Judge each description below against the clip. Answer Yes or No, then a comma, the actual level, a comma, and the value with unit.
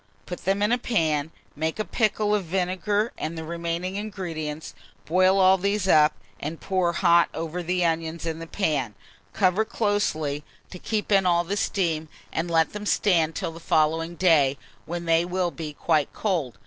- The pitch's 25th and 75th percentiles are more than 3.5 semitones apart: No, average, 3.2 semitones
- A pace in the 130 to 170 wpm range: No, average, 180 wpm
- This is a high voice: No, medium, 170 Hz